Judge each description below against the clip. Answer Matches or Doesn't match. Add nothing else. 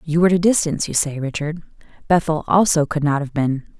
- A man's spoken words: Doesn't match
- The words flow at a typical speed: Doesn't match